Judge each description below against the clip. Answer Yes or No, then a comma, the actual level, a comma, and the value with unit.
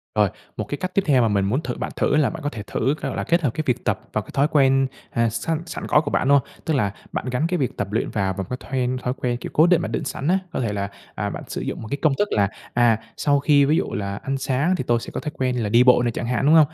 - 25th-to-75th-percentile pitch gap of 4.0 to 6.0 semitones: Yes, average, 4.3 semitones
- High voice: No, low, 130 Hz